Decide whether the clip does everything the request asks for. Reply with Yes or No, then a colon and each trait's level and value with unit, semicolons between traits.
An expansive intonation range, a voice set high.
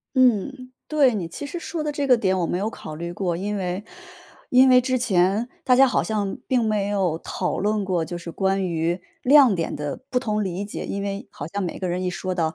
Yes: wide, 5.8 semitones; high, 200 Hz